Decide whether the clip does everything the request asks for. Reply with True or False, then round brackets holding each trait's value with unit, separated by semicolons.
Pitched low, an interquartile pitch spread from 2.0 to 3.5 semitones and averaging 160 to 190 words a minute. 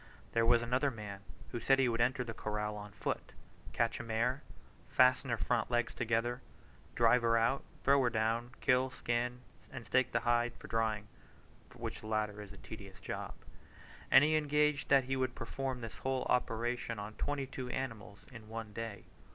True (120 Hz; 2.5 semitones; 180 wpm)